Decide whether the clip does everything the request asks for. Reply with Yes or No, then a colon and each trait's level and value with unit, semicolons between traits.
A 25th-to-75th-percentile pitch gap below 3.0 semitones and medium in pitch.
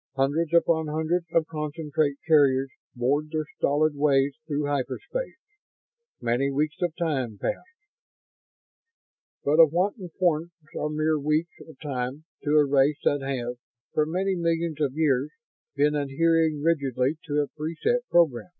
Yes: narrow, 2.6 semitones; medium, 150 Hz